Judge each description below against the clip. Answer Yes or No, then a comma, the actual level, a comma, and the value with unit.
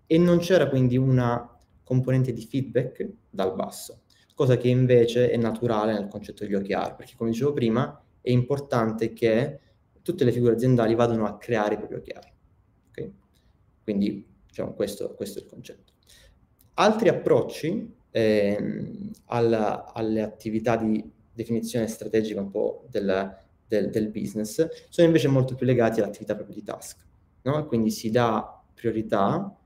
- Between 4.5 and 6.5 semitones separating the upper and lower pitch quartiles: No, average, 2.9 semitones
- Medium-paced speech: Yes, average, 150 wpm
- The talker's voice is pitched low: Yes, low, 115 Hz